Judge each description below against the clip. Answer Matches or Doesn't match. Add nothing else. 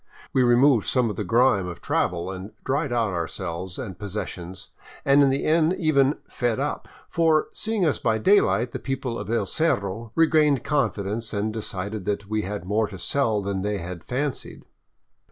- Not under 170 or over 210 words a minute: Matches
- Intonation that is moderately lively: Doesn't match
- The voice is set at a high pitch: Doesn't match